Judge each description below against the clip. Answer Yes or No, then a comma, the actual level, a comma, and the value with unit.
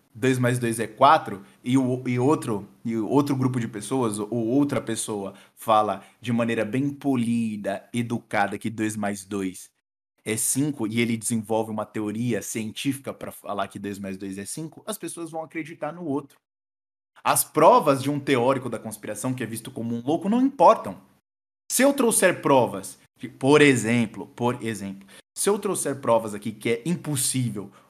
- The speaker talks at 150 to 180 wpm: Yes, average, 170 wpm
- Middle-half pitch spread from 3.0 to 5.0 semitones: Yes, average, 4.6 semitones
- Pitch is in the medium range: No, low, 115 Hz